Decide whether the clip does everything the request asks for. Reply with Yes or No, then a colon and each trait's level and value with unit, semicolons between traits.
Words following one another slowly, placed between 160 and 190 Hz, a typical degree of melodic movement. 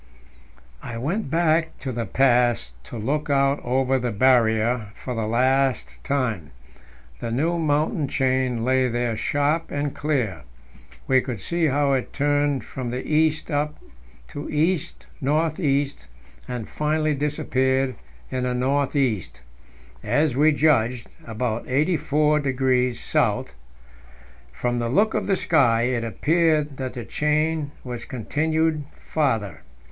No: slow, 130 wpm; low, 135 Hz; average, 3.7 semitones